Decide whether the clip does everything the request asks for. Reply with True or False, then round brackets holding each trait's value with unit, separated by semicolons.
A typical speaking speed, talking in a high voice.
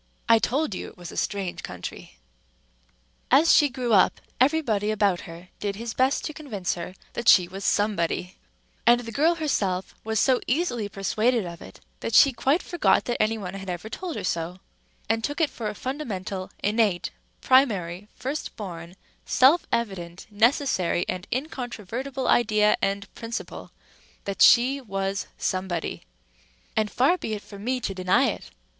True (160 wpm; 215 Hz)